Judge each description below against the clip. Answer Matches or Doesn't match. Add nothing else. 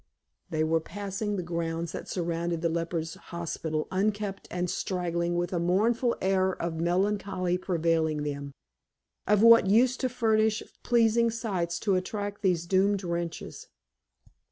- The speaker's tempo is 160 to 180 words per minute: Doesn't match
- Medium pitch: Matches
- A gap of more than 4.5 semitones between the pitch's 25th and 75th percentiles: Doesn't match